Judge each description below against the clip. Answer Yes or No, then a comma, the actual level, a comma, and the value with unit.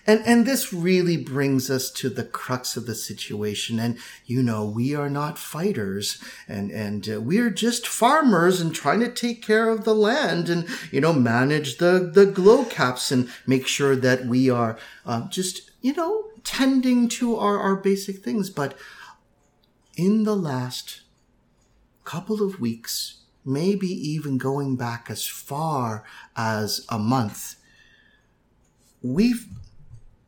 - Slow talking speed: No, average, 145 wpm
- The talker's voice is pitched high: No, medium, 145 Hz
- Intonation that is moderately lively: No, wide, 8.8 semitones